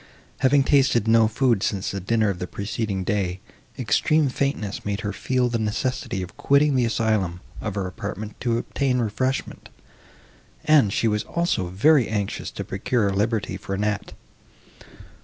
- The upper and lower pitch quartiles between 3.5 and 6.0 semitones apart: Yes, average, 4.4 semitones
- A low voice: Yes, low, 110 Hz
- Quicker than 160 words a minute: No, average, 155 wpm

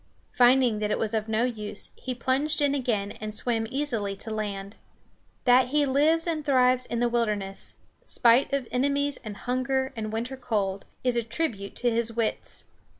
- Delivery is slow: No, average, 175 wpm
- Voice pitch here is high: Yes, high, 240 Hz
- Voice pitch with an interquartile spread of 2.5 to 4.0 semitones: Yes, average, 3.5 semitones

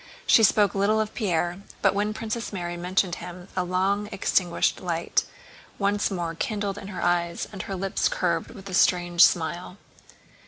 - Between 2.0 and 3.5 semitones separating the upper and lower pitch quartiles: Yes, narrow, 2.6 semitones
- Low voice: No, high, 190 Hz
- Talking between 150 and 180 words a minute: Yes, average, 165 wpm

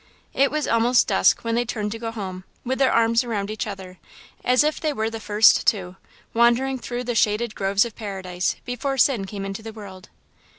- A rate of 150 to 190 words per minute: No, fast, 205 wpm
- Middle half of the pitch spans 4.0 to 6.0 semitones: No, average, 3.4 semitones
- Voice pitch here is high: Yes, high, 225 Hz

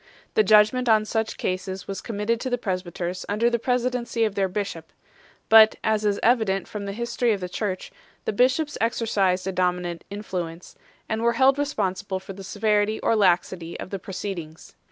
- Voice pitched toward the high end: Yes, high, 205 Hz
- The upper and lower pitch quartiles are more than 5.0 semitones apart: No, average, 3.6 semitones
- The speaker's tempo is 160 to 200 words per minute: Yes, average, 175 wpm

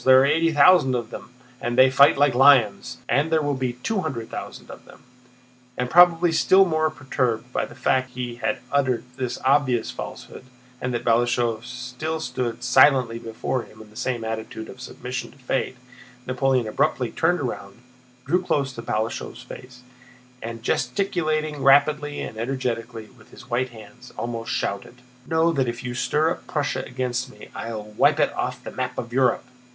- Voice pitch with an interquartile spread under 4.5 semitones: Yes, average, 3.2 semitones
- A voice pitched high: No, low, 130 Hz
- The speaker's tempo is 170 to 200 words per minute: Yes, average, 180 wpm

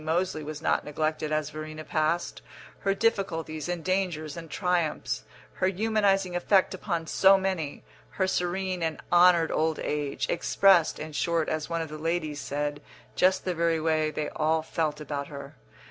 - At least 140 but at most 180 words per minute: Yes, average, 160 wpm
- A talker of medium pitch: Yes, medium, 165 Hz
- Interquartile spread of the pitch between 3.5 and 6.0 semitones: No, average, 2.9 semitones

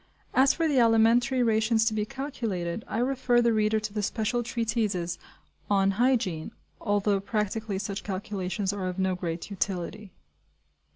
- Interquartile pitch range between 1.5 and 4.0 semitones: Yes, average, 3.3 semitones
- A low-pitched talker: No, high, 215 Hz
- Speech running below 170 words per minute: Yes, average, 150 wpm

